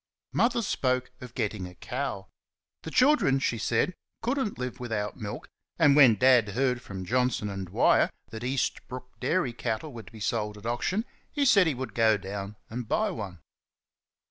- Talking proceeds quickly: No, average, 175 wpm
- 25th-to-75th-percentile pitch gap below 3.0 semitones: No, average, 4.6 semitones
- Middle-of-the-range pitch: No, low, 125 Hz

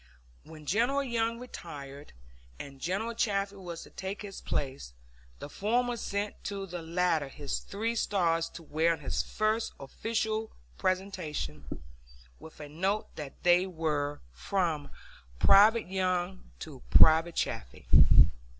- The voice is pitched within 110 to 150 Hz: No, medium, 180 Hz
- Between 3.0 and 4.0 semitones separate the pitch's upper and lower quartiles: No, average, 5.1 semitones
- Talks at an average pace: No, slow, 130 wpm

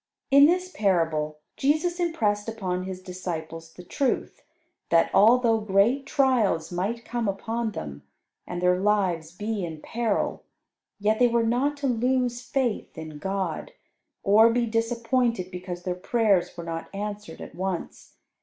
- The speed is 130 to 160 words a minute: Yes, average, 145 wpm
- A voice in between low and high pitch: No, high, 210 Hz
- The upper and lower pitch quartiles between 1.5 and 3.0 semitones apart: No, average, 5.0 semitones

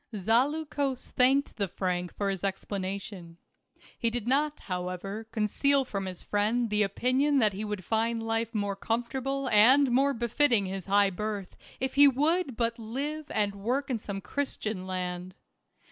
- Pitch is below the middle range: No, high, 225 Hz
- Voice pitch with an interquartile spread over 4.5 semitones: Yes, average, 5.1 semitones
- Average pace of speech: Yes, average, 155 wpm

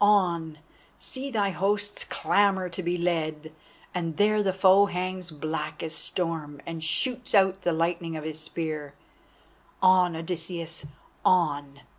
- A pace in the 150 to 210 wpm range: No, slow, 135 wpm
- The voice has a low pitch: No, medium, 175 Hz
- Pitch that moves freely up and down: No, average, 3.1 semitones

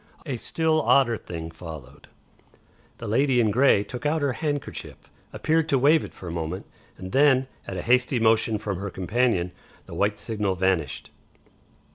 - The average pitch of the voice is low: Yes, low, 115 Hz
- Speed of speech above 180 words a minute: No, average, 165 wpm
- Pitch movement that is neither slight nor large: No, wide, 6.5 semitones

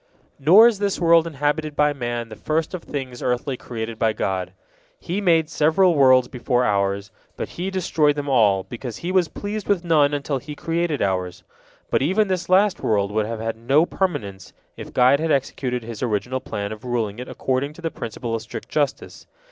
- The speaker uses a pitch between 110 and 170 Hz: Yes, low, 135 Hz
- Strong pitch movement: Yes, wide, 6.2 semitones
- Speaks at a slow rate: No, average, 195 wpm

